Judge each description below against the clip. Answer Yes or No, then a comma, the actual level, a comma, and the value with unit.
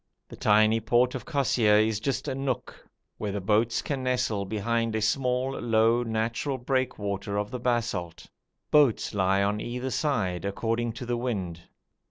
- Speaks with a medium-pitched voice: No, low, 115 Hz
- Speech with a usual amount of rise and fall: Yes, average, 3.3 semitones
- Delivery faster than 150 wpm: Yes, average, 160 wpm